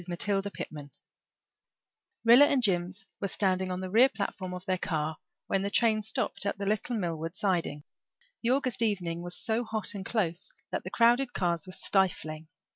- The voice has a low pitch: No, high, 195 Hz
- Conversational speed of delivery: Yes, average, 175 wpm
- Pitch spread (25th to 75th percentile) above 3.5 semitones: Yes, average, 3.9 semitones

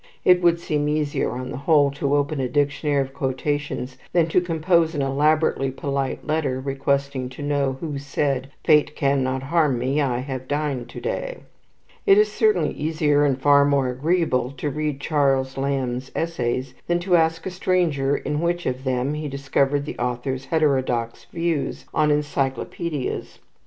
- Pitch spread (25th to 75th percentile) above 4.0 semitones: No, average, 2.7 semitones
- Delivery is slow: No, average, 165 wpm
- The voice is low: No, medium, 145 Hz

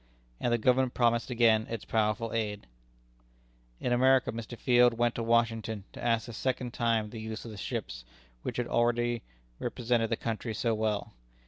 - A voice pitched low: Yes, low, 115 Hz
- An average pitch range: No, narrow, 1.4 semitones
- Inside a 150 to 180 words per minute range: Yes, average, 170 wpm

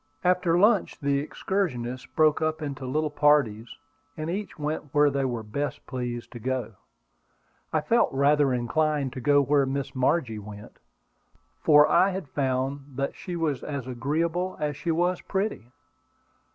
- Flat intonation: No, average, 3.5 semitones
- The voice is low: No, medium, 145 Hz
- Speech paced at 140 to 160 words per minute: Yes, average, 150 wpm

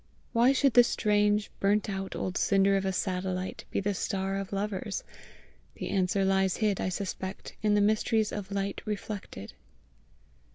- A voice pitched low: No, high, 200 Hz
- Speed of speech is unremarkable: Yes, average, 160 wpm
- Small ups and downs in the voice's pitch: Yes, narrow, 1.5 semitones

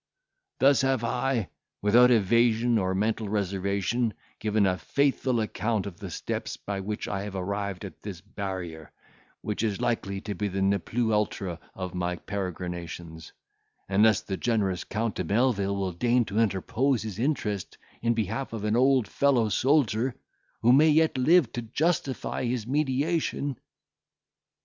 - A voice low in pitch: Yes, low, 110 Hz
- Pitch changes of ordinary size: Yes, average, 4.0 semitones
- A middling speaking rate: Yes, average, 150 wpm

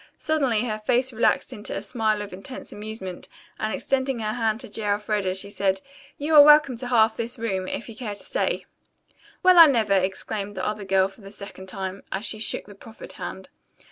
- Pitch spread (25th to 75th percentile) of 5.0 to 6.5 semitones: No, average, 3.5 semitones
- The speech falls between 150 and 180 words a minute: No, fast, 205 wpm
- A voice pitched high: Yes, high, 215 Hz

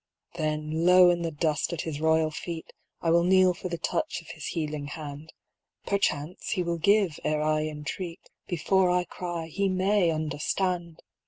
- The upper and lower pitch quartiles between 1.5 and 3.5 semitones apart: Yes, average, 2.8 semitones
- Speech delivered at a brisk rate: No, average, 175 wpm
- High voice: No, medium, 165 Hz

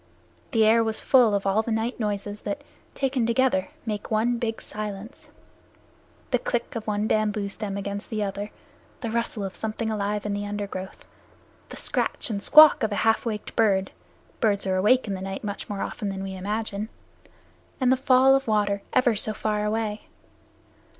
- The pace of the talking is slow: No, average, 180 wpm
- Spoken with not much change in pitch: Yes, narrow, 2.1 semitones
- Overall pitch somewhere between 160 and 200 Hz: No, high, 215 Hz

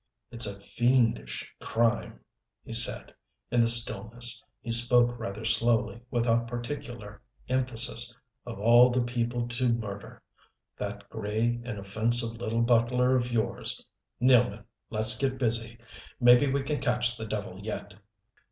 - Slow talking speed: Yes, slow, 130 wpm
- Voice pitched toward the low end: Yes, low, 120 Hz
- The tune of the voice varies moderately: No, narrow, 1.7 semitones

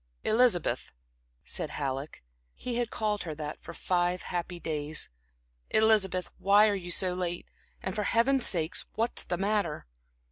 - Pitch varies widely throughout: No, average, 4.0 semitones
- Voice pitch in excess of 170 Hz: Yes, medium, 185 Hz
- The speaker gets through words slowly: No, average, 145 wpm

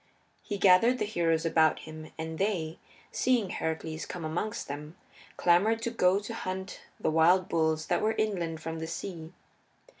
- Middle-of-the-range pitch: Yes, medium, 170 Hz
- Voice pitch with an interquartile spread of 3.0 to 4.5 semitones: Yes, average, 4.0 semitones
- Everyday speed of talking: Yes, average, 160 wpm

